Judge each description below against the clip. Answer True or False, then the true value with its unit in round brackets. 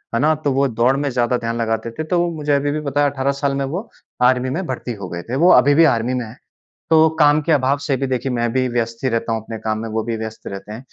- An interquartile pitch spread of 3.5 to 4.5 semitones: True (3.8 semitones)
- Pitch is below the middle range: True (130 Hz)